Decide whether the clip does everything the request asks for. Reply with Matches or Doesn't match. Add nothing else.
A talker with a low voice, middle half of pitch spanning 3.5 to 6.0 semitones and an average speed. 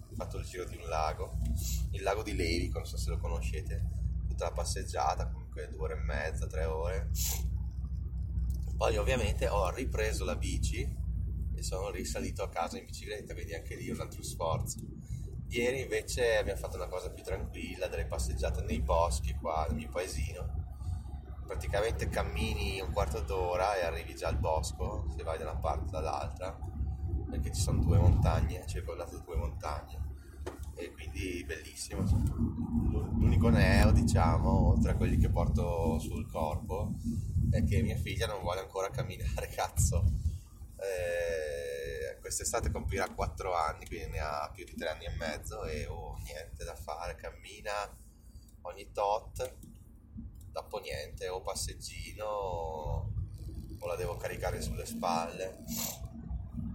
Matches